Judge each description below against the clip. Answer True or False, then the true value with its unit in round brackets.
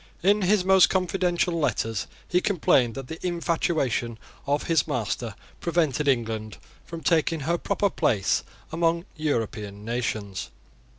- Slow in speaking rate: True (125 wpm)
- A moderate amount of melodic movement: False (6.9 semitones)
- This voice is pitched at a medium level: True (160 Hz)